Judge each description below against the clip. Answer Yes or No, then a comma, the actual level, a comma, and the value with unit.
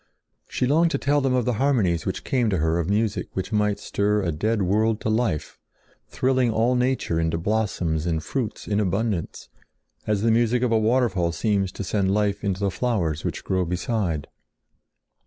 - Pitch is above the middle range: No, low, 105 Hz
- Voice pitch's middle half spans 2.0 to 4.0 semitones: No, average, 4.4 semitones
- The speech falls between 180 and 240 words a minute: Yes, average, 185 wpm